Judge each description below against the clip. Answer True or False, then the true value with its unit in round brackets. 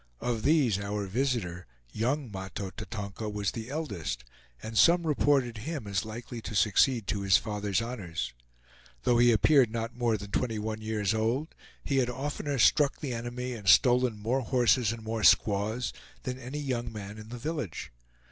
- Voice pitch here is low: True (115 Hz)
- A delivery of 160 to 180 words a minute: True (170 wpm)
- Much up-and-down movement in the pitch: False (3.5 semitones)